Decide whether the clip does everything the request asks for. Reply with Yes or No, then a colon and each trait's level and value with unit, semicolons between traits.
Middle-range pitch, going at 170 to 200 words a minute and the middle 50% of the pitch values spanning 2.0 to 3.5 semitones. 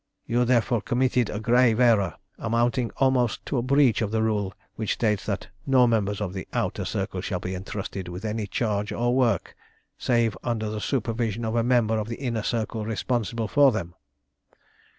No: low, 115 Hz; average, 180 wpm; narrow, 2.4 semitones